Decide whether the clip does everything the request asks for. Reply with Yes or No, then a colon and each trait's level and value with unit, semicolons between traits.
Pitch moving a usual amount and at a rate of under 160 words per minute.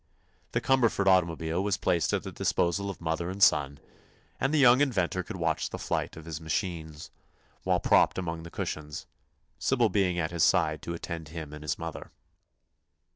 No: average, 3.5 semitones; average, 180 wpm